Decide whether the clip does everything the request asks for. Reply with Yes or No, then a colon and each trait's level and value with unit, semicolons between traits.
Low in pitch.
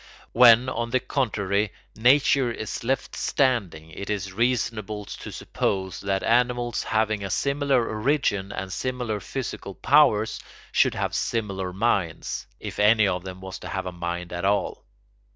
Yes: low, 110 Hz